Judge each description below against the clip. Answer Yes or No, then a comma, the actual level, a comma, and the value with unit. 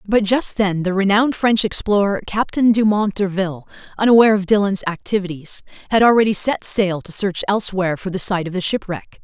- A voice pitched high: Yes, high, 200 Hz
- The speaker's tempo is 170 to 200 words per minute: Yes, average, 175 wpm